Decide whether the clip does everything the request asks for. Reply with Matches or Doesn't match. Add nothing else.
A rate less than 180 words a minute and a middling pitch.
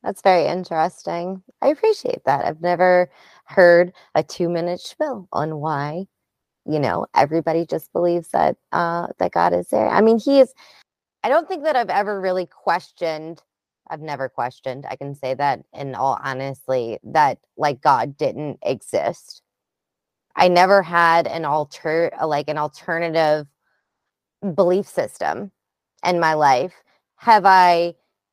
Matches